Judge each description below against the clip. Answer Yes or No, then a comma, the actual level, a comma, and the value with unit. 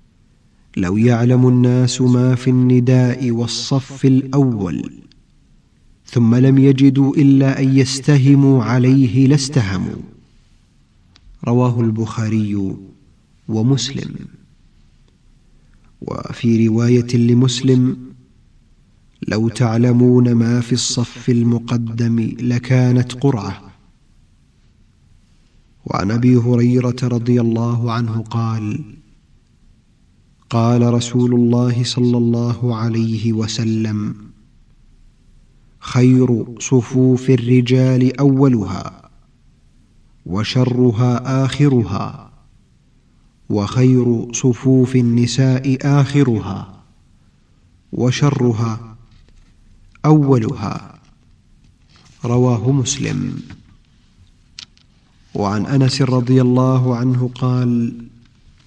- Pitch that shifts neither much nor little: No, narrow, 2.1 semitones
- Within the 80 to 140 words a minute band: No, slow, 65 wpm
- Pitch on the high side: No, low, 125 Hz